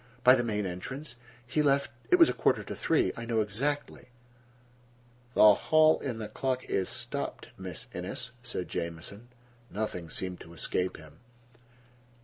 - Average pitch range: No, wide, 6.3 semitones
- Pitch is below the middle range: Yes, low, 115 Hz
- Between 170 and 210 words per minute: No, average, 145 wpm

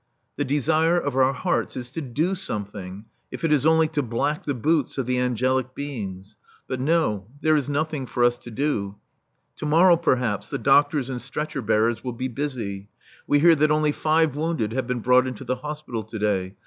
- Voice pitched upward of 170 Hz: No, low, 130 Hz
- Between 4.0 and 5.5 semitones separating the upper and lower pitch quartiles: Yes, average, 4.6 semitones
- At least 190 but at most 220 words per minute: Yes, average, 200 wpm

